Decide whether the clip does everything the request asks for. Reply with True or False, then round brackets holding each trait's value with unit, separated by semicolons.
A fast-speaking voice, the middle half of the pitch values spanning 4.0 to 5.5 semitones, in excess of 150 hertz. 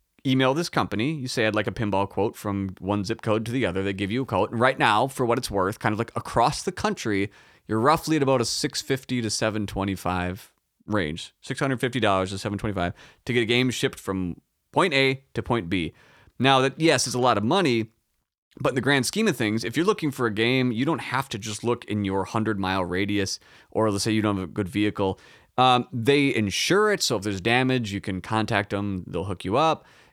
False (230 wpm; 4.4 semitones; 110 Hz)